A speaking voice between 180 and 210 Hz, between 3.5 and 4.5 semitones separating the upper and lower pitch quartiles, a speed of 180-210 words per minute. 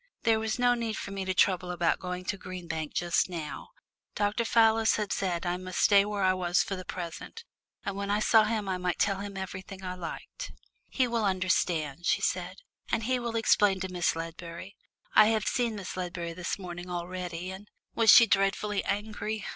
No: high, 190 Hz; average, 3.1 semitones; fast, 205 wpm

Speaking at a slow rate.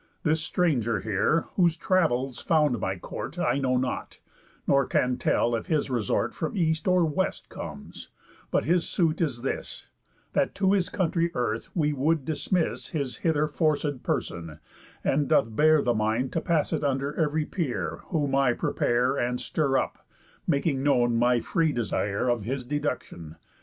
No: average, 165 wpm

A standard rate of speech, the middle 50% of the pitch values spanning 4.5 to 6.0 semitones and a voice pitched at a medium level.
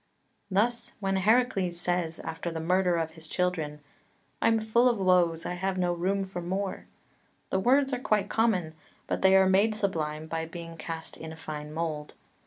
No: average, 185 wpm; average, 3.4 semitones; medium, 180 Hz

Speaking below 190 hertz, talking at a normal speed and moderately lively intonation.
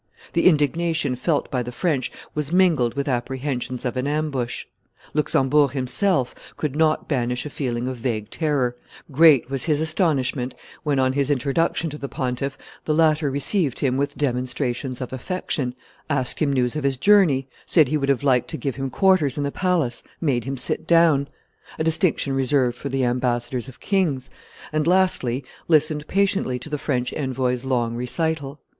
Yes: medium, 140 Hz; average, 170 wpm; average, 3.4 semitones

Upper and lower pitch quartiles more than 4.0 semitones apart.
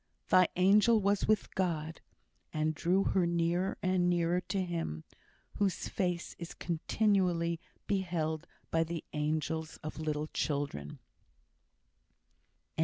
No: average, 2.8 semitones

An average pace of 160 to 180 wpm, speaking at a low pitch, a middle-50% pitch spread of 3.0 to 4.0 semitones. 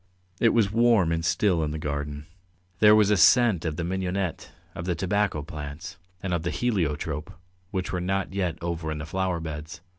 No: average, 190 wpm; very low, 85 Hz; average, 3.7 semitones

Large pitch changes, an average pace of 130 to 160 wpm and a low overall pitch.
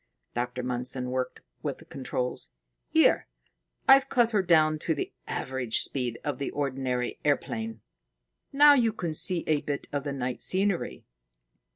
No: wide, 6.9 semitones; average, 150 wpm; medium, 145 Hz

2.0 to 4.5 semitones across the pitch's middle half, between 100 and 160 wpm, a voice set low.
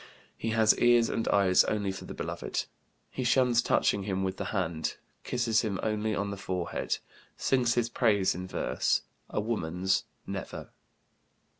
Yes: average, 3.4 semitones; average, 155 wpm; low, 105 Hz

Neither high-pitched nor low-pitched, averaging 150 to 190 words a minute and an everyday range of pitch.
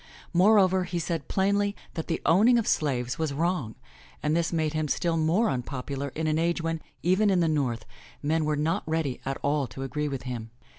No: medium, 160 Hz; average, 200 wpm; average, 3.7 semitones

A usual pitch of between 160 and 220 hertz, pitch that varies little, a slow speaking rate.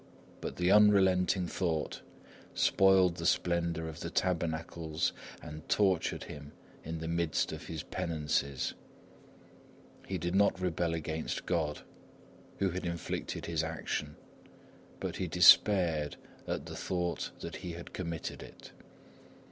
No: very low, 85 Hz; narrow, 2.3 semitones; slow, 125 wpm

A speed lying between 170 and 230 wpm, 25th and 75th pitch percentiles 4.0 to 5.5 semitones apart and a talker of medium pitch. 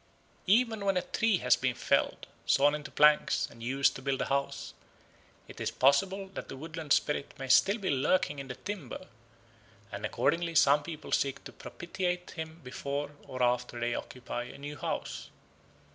Yes: average, 175 wpm; average, 4.9 semitones; medium, 145 Hz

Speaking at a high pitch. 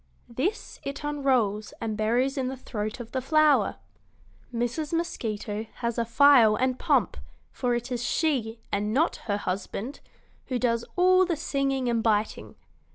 Yes: high, 245 Hz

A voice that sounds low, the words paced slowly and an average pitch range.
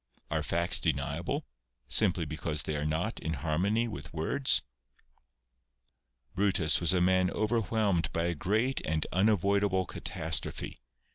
Yes: very low, 90 Hz; slow, 125 wpm; average, 4.4 semitones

